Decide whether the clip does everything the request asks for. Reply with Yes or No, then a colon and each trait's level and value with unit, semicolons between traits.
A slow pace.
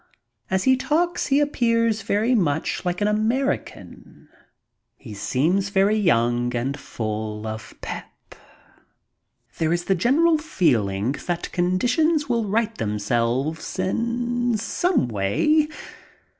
Yes: slow, 130 wpm